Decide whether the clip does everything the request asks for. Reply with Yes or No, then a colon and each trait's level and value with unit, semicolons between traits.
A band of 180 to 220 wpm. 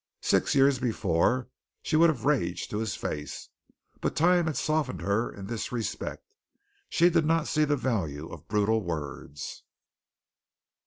No: average, 150 wpm